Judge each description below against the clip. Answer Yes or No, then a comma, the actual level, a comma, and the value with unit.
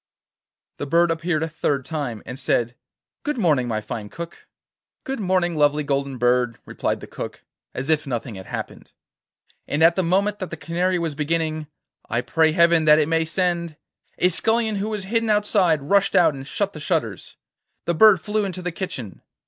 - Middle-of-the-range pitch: Yes, medium, 165 Hz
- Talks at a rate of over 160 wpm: Yes, average, 185 wpm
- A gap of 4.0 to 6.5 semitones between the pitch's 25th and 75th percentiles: Yes, average, 4.6 semitones